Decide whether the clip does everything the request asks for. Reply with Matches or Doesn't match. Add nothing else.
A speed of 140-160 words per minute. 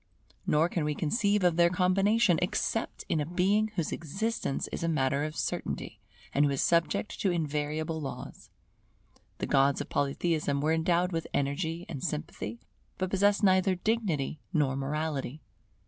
Matches